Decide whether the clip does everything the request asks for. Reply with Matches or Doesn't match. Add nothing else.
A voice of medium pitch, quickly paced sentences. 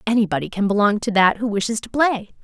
Doesn't match